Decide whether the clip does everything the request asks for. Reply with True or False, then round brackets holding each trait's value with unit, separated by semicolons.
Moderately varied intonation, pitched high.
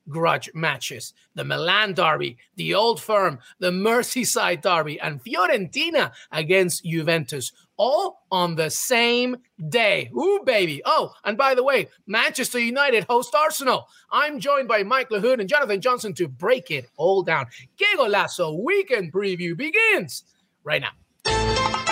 False (8.1 semitones; 220 Hz)